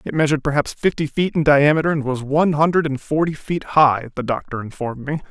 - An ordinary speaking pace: No, fast, 215 wpm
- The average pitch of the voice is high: No, medium, 145 Hz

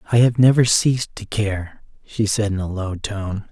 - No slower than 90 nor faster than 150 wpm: No, fast, 205 wpm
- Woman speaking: No, male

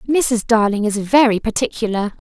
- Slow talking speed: Yes, slow, 130 wpm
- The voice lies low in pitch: No, high, 225 Hz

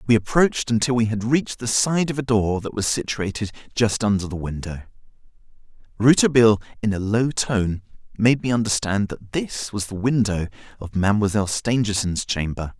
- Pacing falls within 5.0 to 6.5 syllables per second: Yes, 5.5 syllables/s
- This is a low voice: Yes, low, 110 Hz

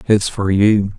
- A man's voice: Yes, male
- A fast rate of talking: No, average, 185 wpm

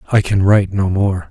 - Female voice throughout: No, male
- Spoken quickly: Yes, fast, 230 wpm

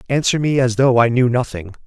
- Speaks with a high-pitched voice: No, low, 125 Hz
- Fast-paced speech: Yes, fast, 225 wpm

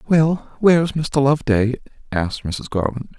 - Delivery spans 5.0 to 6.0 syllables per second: No, 4.7 syllables/s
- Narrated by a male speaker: Yes, male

